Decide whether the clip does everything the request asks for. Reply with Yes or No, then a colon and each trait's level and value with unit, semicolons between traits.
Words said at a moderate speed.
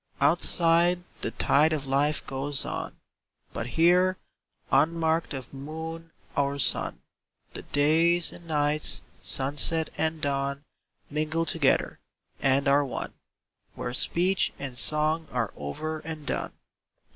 No: slow, 120 wpm